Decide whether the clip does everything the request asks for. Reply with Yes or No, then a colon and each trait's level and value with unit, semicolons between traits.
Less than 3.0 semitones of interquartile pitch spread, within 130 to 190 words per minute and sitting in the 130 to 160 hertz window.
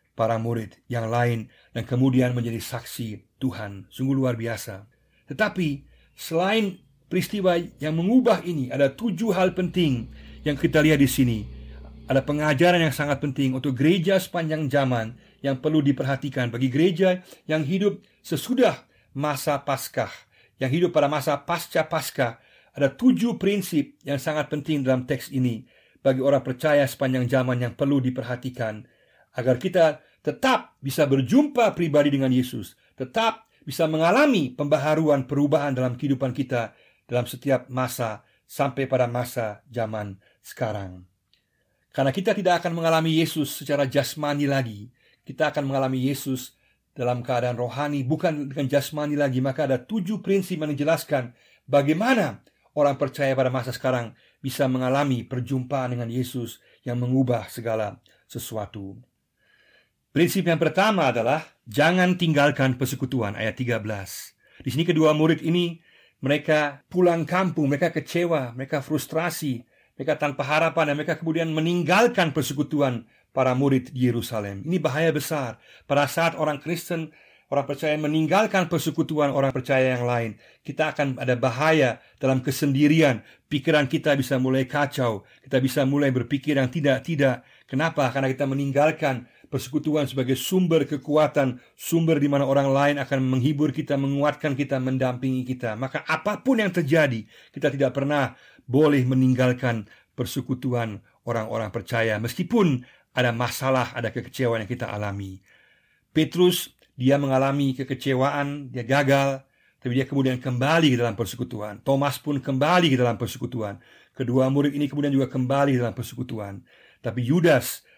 No: average, 3.5 semitones; average, 135 wpm; medium, 140 Hz